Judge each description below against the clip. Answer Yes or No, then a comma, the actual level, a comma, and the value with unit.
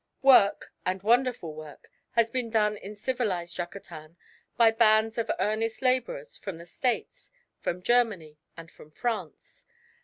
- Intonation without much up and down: No, wide, 5.6 semitones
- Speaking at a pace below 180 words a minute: Yes, slow, 135 wpm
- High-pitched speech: Yes, high, 215 Hz